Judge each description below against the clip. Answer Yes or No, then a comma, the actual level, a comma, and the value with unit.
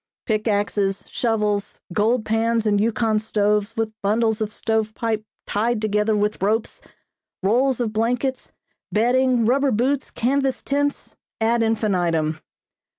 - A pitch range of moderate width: No, narrow, 2.2 semitones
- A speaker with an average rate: No, slow, 125 wpm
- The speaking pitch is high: Yes, high, 220 Hz